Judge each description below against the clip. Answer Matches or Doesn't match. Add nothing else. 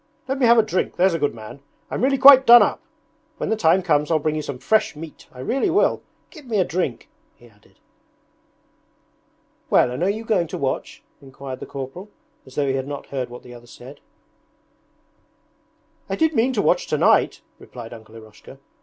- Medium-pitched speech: Matches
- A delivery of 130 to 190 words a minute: Doesn't match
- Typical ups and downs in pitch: Doesn't match